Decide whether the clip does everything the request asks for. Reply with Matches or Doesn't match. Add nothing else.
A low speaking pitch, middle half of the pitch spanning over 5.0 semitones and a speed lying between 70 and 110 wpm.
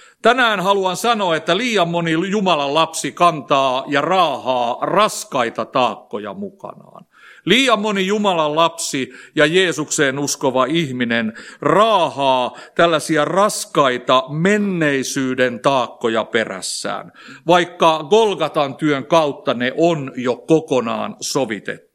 Doesn't match